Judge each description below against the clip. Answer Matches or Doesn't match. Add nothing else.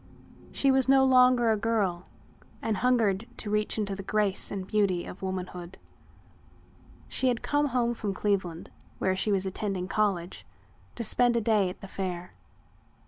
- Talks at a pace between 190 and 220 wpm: Doesn't match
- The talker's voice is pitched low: Doesn't match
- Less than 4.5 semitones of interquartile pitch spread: Matches